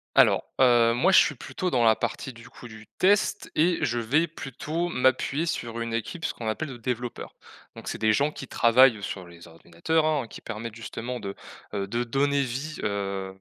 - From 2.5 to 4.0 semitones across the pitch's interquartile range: No, average, 4.5 semitones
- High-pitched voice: No, low, 120 Hz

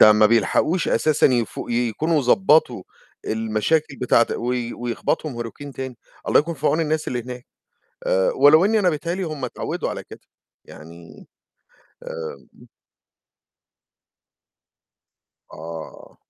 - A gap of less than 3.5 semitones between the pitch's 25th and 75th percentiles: No, wide, 5.6 semitones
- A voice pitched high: No, low, 125 Hz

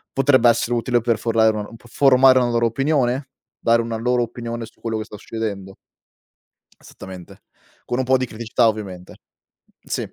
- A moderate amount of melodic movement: No, narrow, 2.1 semitones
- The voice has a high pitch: No, low, 115 Hz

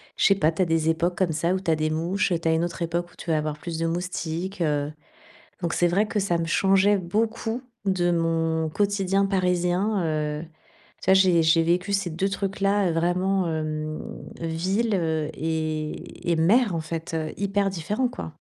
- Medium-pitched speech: Yes, medium, 175 Hz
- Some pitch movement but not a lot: Yes, average, 3.2 semitones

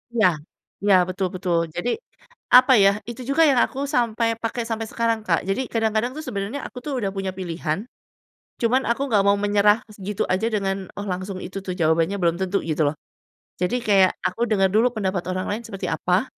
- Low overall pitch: No, high, 205 Hz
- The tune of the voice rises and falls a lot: No, average, 3.7 semitones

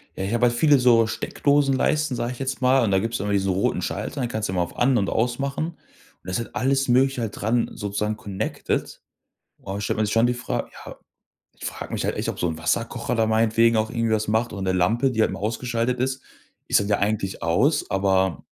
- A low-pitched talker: Yes, low, 115 Hz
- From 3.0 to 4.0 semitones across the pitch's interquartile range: Yes, average, 3.6 semitones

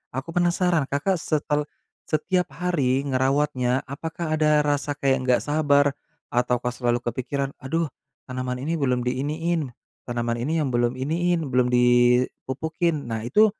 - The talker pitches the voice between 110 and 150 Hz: Yes, medium, 140 Hz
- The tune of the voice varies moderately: Yes, average, 3.9 semitones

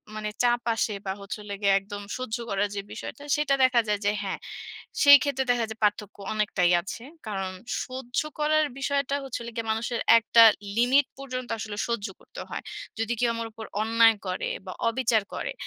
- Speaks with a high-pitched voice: Yes, high, 230 Hz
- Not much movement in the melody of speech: No, average, 3.5 semitones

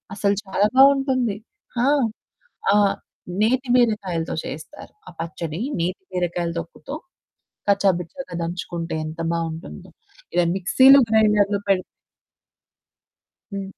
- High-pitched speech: Yes, high, 195 Hz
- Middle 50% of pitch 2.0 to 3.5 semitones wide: No, average, 4.4 semitones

